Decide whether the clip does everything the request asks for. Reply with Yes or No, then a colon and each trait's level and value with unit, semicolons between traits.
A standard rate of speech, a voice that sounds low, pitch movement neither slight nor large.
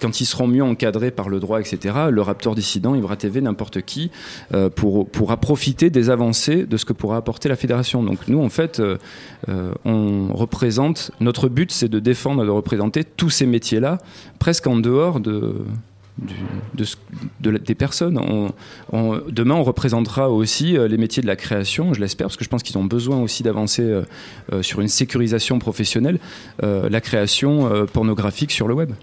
Yes: average, 190 wpm; low, 115 Hz; average, 3.9 semitones